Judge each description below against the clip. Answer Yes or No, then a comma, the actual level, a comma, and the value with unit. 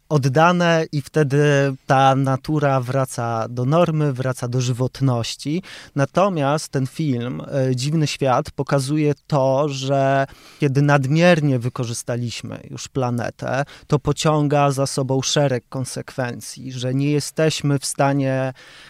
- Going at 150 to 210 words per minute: No, slow, 110 wpm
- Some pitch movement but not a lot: No, narrow, 2.1 semitones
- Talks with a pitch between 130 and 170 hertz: Yes, medium, 140 Hz